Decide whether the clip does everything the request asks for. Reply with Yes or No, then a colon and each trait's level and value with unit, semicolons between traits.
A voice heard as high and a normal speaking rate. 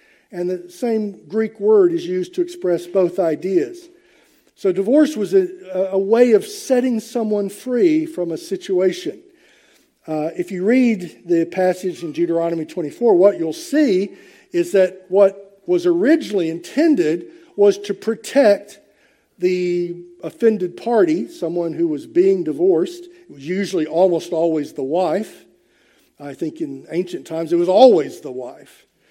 Yes: high, 205 Hz; average, 145 wpm